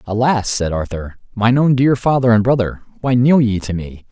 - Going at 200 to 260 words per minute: Yes, fast, 205 wpm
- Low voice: Yes, low, 115 Hz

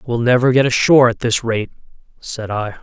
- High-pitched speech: No, low, 120 Hz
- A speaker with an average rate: Yes, average, 190 wpm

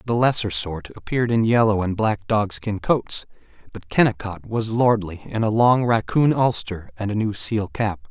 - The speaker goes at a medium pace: Yes, average, 180 wpm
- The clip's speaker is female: No, male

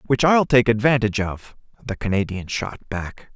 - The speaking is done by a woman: No, male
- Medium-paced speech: Yes, average, 160 wpm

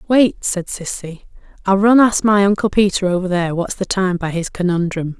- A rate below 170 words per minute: No, average, 195 wpm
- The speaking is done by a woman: Yes, female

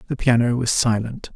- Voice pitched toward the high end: No, low, 120 Hz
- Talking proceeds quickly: No, average, 180 wpm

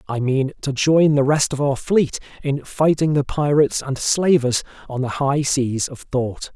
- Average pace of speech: Yes, average, 190 wpm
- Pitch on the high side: No, medium, 140 Hz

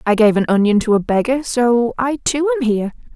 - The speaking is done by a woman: Yes, female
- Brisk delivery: Yes, fast, 230 wpm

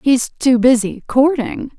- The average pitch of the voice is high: Yes, very high, 250 Hz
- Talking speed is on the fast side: No, slow, 135 wpm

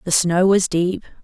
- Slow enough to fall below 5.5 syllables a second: Yes, 4.3 syllables/s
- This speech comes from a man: No, female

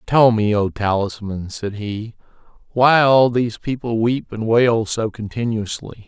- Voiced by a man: Yes, male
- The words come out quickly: No, average, 150 wpm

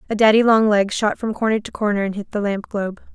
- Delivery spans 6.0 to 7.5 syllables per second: Yes, 6.3 syllables/s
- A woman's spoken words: Yes, female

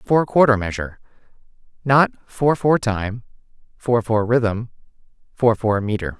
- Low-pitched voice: Yes, low, 115 Hz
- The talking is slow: Yes, slow, 125 wpm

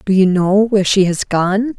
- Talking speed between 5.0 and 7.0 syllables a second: No, 4.7 syllables/s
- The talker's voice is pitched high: Yes, high, 195 Hz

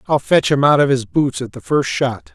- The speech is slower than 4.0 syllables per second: No, 4.9 syllables/s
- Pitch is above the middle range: No, low, 135 Hz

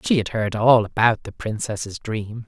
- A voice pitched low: Yes, low, 110 Hz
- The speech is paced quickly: No, average, 195 wpm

